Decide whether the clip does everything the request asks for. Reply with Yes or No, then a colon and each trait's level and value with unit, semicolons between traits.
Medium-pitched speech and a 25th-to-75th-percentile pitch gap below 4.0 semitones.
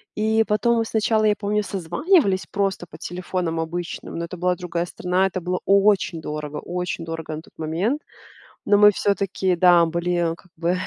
Yes: medium, 180 Hz; average, 3.3 semitones